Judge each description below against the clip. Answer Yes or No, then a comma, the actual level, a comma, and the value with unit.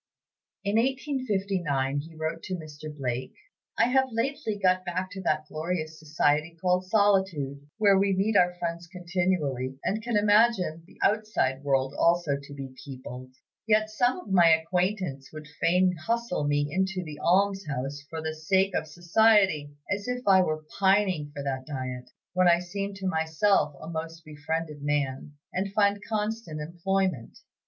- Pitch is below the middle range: No, medium, 175 Hz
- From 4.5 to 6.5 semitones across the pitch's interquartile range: Yes, average, 4.9 semitones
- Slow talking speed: No, average, 155 wpm